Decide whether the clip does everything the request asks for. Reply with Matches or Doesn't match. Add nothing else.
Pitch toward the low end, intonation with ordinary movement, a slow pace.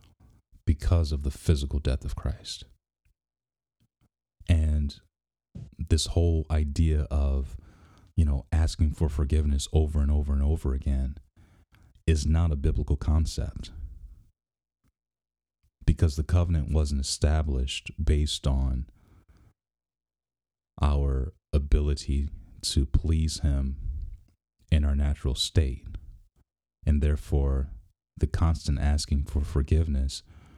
Matches